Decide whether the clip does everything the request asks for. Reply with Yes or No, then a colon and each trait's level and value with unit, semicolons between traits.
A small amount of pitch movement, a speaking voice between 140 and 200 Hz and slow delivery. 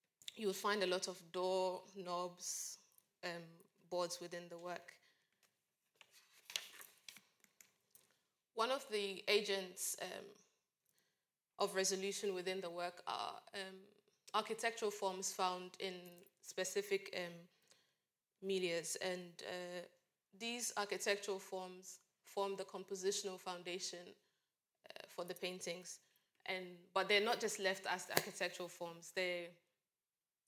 Yes: narrow, 1.8 semitones; medium, 185 Hz; slow, 110 wpm